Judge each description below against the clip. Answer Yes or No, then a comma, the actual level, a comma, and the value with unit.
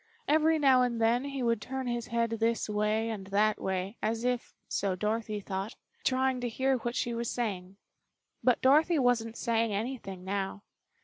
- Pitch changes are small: No, average, 3.1 semitones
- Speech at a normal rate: Yes, average, 175 wpm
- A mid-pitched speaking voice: No, high, 230 Hz